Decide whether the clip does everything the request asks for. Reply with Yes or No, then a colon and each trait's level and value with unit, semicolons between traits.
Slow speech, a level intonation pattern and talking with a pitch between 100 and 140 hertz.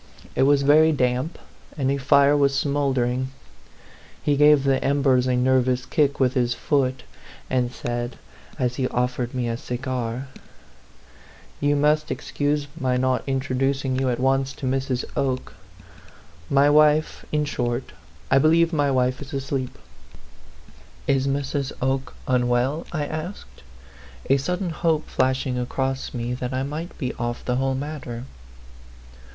No: average, 145 wpm; narrow, 2.2 semitones; low, 135 Hz